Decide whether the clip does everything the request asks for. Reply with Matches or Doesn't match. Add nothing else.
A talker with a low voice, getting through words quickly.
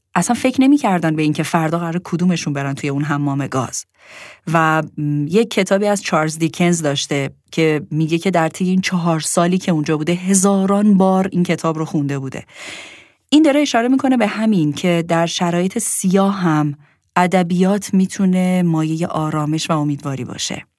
Doesn't match